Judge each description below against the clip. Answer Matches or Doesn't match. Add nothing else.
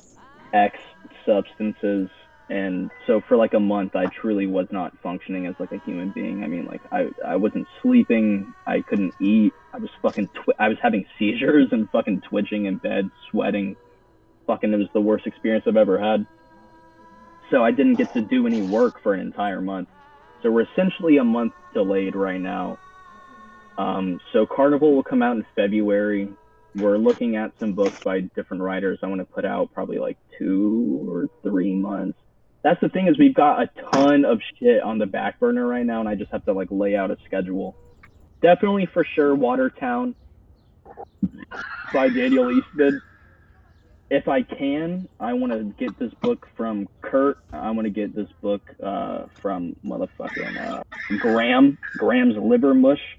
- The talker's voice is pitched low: Matches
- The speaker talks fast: Doesn't match